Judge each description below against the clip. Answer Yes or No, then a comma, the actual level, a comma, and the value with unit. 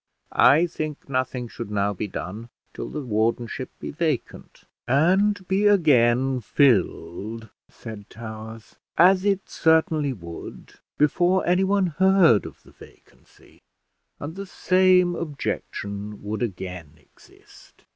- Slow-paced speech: Yes, slow, 115 wpm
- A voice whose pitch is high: No, low, 135 Hz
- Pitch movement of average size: No, wide, 8.3 semitones